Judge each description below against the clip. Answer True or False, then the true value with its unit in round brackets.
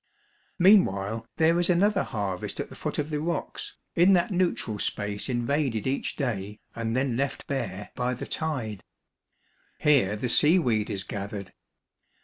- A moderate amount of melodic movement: False (7.2 semitones)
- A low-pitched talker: True (125 Hz)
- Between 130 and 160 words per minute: True (145 wpm)